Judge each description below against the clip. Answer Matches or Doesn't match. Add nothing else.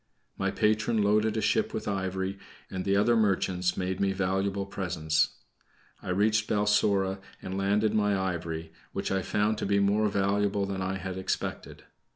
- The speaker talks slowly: Doesn't match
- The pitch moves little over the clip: Matches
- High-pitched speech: Doesn't match